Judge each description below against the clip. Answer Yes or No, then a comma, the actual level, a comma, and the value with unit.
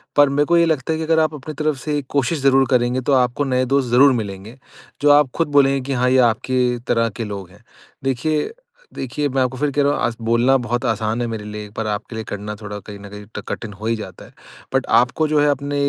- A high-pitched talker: No, low, 125 Hz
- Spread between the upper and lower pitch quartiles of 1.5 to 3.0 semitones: No, average, 4.3 semitones